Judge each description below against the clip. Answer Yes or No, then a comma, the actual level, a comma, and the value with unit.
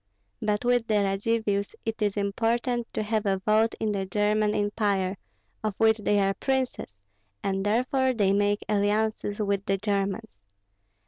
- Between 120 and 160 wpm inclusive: Yes, average, 150 wpm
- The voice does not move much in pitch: Yes, narrow, 1.9 semitones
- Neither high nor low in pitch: No, high, 210 Hz